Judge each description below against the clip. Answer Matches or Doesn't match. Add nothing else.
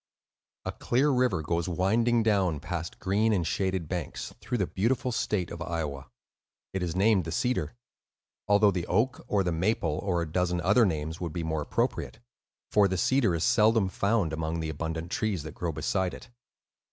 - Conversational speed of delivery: Matches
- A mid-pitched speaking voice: Doesn't match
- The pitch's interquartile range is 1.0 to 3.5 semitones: Doesn't match